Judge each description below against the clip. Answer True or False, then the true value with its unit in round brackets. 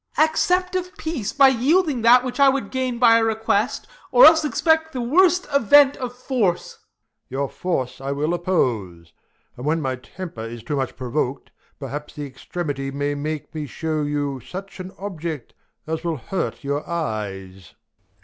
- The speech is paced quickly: False (170 wpm)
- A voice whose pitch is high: False (170 Hz)